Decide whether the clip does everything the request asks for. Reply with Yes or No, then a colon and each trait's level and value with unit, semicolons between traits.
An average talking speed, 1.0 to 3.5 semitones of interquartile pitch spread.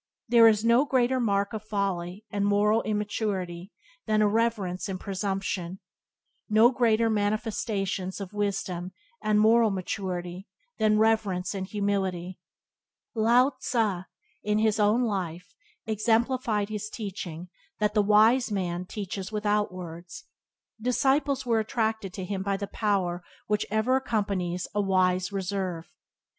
No: slow, 125 wpm; average, 2.8 semitones